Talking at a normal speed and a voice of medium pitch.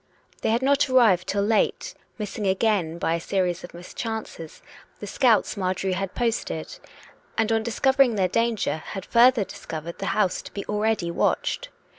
No: average, 160 wpm; high, 205 Hz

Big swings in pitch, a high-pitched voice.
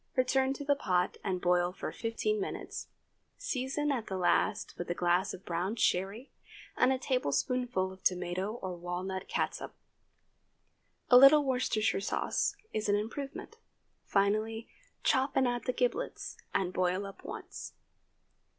Yes: wide, 5.9 semitones; high, 215 Hz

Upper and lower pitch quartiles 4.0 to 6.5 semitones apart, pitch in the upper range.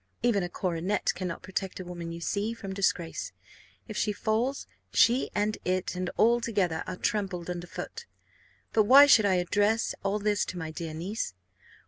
No: average, 3.3 semitones; high, 195 Hz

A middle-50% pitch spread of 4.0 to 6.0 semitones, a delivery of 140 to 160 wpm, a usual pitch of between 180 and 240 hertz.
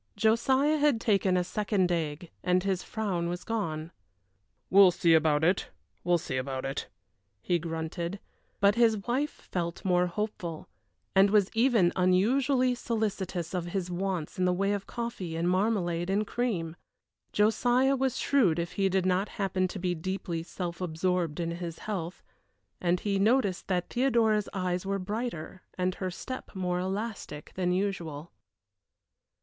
No: average, 3.5 semitones; average, 150 wpm; medium, 185 Hz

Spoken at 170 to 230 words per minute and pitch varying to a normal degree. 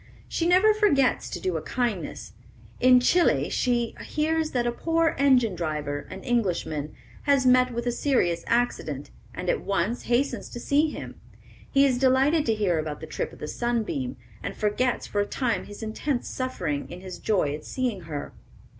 No: average, 180 wpm; wide, 6.5 semitones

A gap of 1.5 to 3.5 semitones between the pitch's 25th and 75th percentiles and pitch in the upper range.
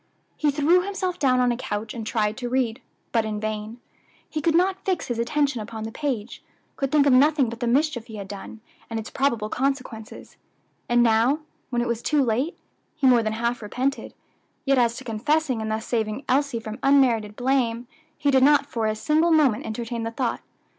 No: average, 4.0 semitones; high, 245 Hz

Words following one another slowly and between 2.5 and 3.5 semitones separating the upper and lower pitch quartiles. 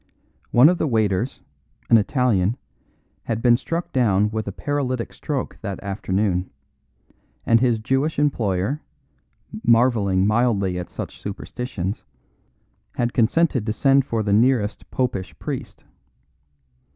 No: slow, 120 wpm; average, 4.3 semitones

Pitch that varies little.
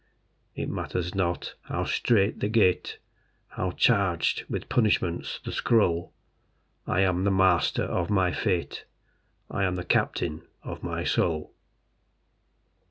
Yes: narrow, 2.3 semitones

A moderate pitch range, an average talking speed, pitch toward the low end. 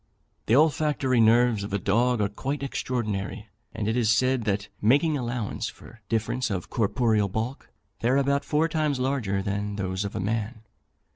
Yes: average, 4.1 semitones; average, 170 wpm; low, 115 Hz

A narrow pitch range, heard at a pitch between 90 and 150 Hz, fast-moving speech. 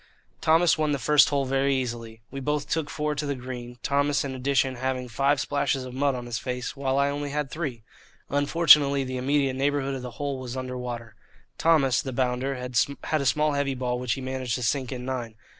Yes: narrow, 2.2 semitones; low, 135 Hz; fast, 210 wpm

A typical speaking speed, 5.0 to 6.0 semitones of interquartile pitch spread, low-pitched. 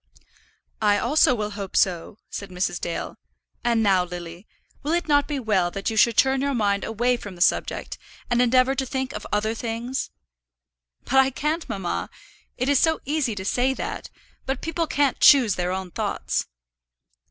No: average, 175 wpm; average, 5.3 semitones; high, 235 Hz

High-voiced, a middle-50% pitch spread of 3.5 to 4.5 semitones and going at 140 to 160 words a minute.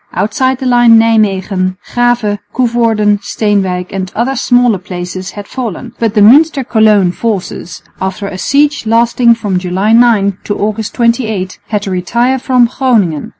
Yes: high, 215 Hz; average, 3.9 semitones; average, 150 wpm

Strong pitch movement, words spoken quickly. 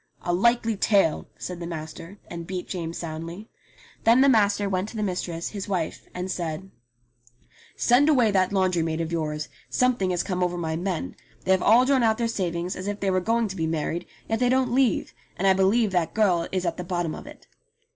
No: average, 4.3 semitones; fast, 215 wpm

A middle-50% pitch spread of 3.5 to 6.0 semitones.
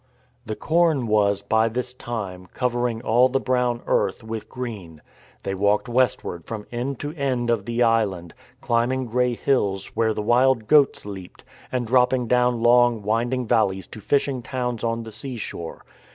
No: average, 2.7 semitones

